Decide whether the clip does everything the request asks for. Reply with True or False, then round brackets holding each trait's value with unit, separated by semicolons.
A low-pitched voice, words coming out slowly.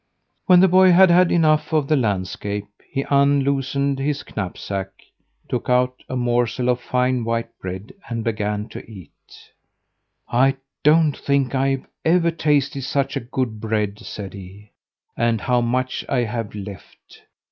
False (125 Hz; 145 wpm)